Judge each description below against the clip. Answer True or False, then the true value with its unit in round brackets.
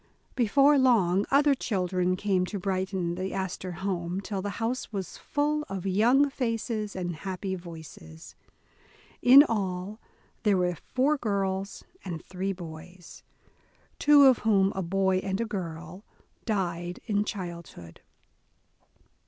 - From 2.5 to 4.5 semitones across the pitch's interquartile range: True (3.4 semitones)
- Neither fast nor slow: False (130 wpm)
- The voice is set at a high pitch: True (195 Hz)